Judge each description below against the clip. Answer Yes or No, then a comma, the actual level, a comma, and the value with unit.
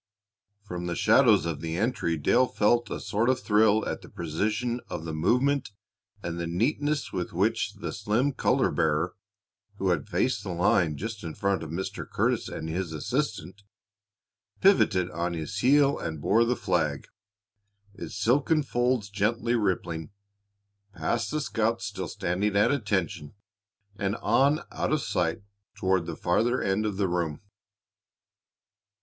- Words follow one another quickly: No, average, 150 wpm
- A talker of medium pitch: No, low, 100 Hz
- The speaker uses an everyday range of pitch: No, wide, 5.7 semitones